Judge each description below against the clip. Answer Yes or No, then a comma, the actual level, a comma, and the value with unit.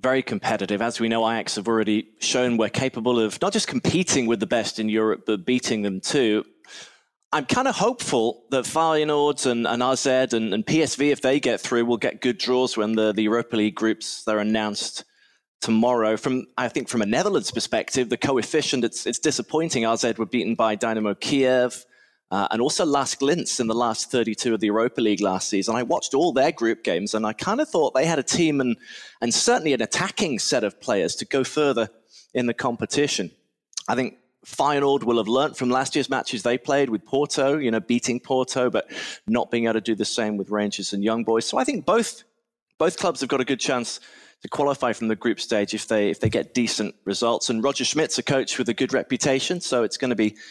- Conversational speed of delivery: No, fast, 220 wpm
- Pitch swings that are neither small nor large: Yes, average, 3.4 semitones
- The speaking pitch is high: No, low, 120 Hz